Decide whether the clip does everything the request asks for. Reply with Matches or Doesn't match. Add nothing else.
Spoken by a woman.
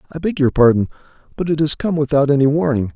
Doesn't match